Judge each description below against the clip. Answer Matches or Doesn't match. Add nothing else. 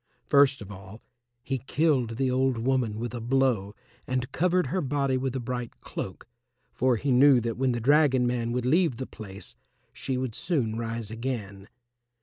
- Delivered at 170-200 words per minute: Matches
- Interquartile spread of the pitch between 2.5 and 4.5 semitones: Matches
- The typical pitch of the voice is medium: Doesn't match